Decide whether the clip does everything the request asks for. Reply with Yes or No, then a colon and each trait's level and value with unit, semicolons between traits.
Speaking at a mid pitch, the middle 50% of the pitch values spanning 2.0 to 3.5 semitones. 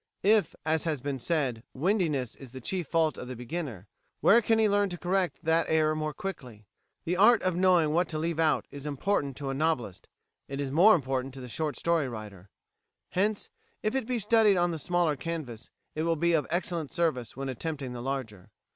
No: medium, 155 Hz; average, 5.0 semitones